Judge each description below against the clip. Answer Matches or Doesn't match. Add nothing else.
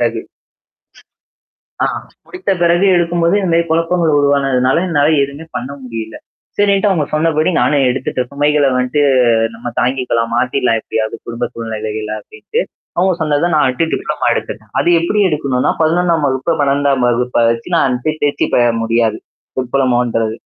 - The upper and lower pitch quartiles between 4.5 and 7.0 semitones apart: Matches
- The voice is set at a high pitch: Doesn't match